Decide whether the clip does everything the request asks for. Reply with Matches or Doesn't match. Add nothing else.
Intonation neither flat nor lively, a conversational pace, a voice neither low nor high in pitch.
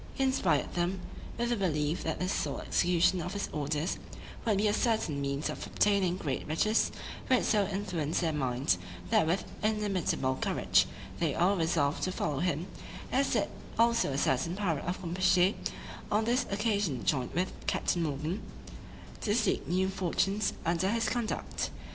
Matches